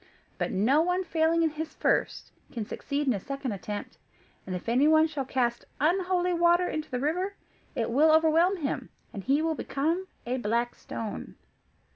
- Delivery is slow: No, average, 170 wpm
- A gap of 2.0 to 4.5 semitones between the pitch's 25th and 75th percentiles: No, wide, 5.4 semitones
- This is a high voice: Yes, very high, 300 Hz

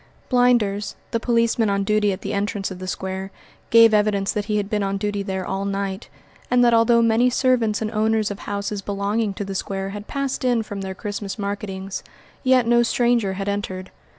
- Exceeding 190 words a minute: Yes, average, 200 wpm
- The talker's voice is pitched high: Yes, high, 205 Hz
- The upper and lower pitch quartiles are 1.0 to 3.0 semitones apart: Yes, narrow, 2.6 semitones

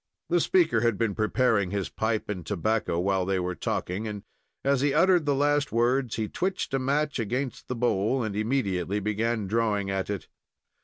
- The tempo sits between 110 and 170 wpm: No, average, 185 wpm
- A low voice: Yes, low, 110 Hz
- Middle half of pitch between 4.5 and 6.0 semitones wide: Yes, average, 5.1 semitones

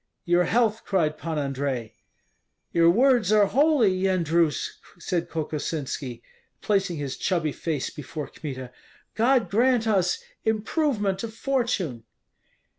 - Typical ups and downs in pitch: No, wide, 6.5 semitones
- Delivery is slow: Yes, slow, 115 wpm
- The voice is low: No, medium, 180 Hz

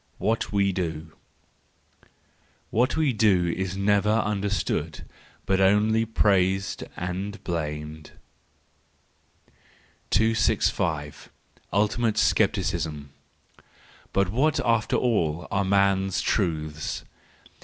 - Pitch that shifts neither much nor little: Yes, average, 3.7 semitones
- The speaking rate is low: Yes, slow, 80 wpm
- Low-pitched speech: Yes, low, 100 Hz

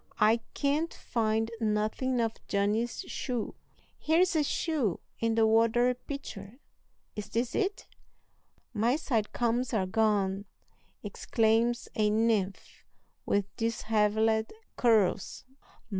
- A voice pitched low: No, high, 225 Hz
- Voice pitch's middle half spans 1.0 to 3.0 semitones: Yes, narrow, 2.4 semitones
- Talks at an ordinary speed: No, slow, 105 wpm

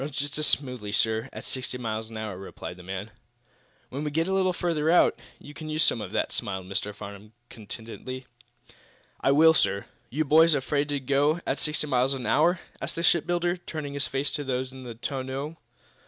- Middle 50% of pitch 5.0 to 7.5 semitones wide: Yes, wide, 5.4 semitones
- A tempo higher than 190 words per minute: Yes, average, 200 wpm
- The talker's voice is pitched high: No, low, 135 Hz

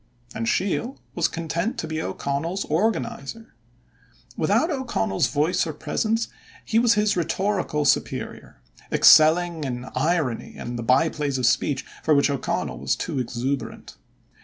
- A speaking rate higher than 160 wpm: No, slow, 135 wpm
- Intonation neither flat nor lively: No, wide, 6.4 semitones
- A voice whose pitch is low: No, medium, 160 Hz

